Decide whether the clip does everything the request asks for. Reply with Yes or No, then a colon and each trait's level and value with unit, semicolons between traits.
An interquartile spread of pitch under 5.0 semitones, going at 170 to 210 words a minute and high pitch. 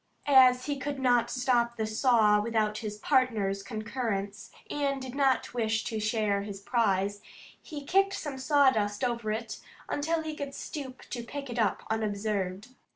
No: average, 4.0 semitones; average, 155 wpm; high, 235 Hz